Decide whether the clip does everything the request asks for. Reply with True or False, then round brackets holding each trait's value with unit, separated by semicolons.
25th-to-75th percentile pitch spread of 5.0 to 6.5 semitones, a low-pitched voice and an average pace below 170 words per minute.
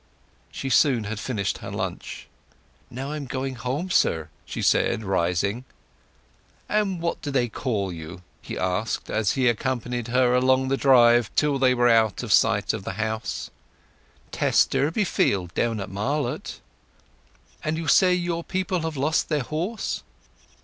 True (5.4 semitones; 125 Hz; 155 wpm)